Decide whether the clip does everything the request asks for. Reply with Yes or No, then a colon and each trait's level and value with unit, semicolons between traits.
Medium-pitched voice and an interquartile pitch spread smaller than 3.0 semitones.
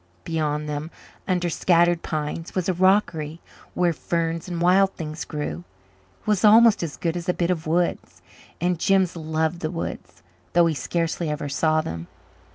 Yes: medium, 165 Hz; narrow, 2.4 semitones